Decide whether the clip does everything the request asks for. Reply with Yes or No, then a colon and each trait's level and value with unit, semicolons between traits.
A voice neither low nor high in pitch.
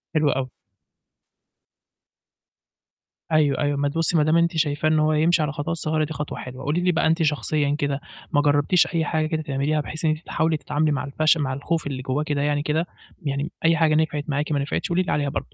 Yes: medium, 150 Hz